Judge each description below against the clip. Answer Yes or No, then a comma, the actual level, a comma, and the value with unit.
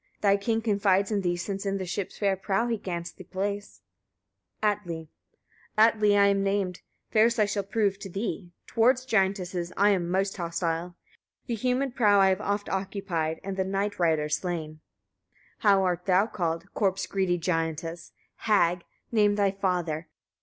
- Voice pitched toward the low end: No, high, 195 Hz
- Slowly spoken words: No, average, 165 wpm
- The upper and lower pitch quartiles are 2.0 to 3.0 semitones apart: Yes, average, 2.7 semitones